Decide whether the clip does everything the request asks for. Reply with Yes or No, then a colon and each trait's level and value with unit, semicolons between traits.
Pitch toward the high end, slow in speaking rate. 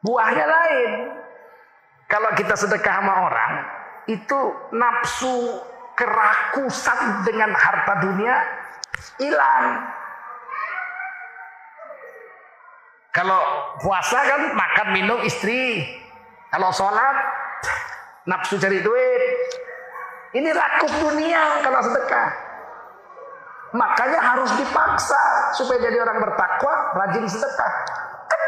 Yes: very high, 275 Hz; slow, 80 wpm